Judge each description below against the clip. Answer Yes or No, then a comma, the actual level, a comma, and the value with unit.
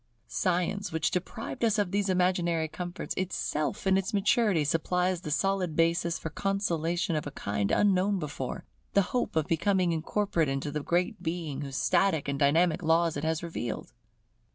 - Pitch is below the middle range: No, medium, 170 Hz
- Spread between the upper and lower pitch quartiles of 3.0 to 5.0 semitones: Yes, average, 3.4 semitones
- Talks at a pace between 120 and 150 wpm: No, average, 165 wpm